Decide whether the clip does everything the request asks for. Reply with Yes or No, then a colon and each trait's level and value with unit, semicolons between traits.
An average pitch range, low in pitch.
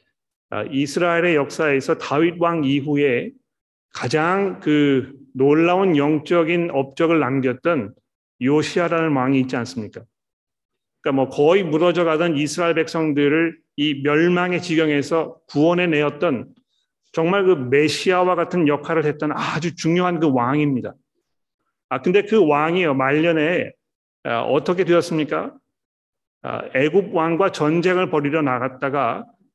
No: average, 3.0 semitones; medium, 160 Hz